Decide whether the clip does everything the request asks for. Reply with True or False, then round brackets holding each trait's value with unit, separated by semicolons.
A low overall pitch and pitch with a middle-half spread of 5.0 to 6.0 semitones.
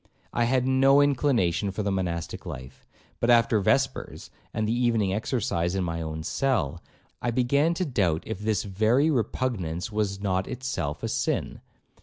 True (110 Hz; 5.5 semitones)